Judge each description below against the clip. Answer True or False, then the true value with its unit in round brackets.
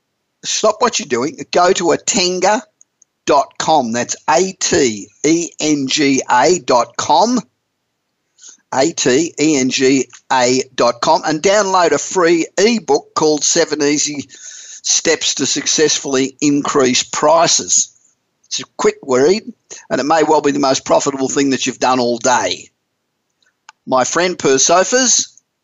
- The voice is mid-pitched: True (150 Hz)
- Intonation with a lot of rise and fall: True (6.1 semitones)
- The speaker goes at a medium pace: False (130 wpm)